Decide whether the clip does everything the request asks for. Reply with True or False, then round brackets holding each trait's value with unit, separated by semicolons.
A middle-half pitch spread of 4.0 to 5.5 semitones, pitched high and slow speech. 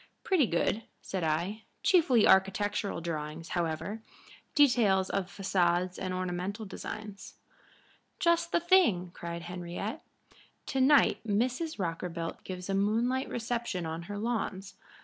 True (5.1 semitones; 195 Hz; 120 wpm)